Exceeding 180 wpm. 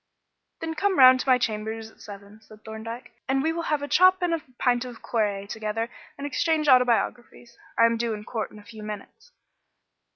Yes: average, 200 wpm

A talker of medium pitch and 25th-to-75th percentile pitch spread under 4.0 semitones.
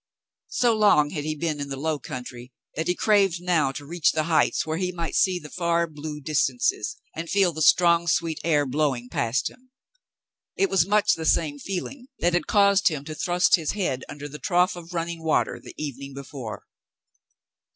Yes: medium, 165 Hz; average, 3.5 semitones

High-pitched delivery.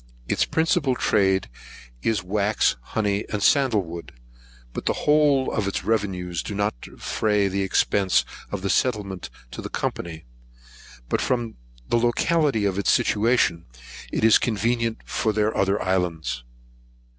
No: low, 105 Hz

